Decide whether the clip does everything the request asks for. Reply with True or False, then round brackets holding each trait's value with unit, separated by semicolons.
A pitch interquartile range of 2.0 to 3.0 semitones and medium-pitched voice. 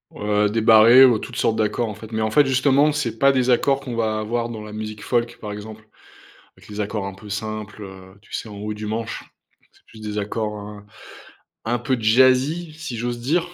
False (2.4 semitones; 110 Hz)